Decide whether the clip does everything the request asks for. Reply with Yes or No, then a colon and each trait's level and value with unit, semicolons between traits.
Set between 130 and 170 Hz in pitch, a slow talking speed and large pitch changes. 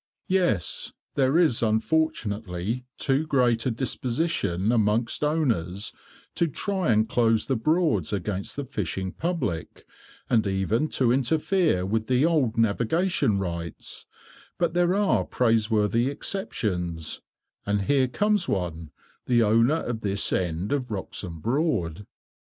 No: low, 115 Hz; slow, 125 wpm; wide, 6.8 semitones